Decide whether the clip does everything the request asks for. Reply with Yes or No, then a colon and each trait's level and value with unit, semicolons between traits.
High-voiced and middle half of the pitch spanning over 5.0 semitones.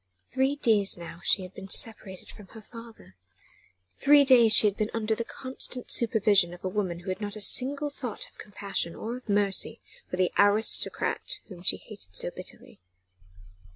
No: high, 210 Hz; average, 3.5 semitones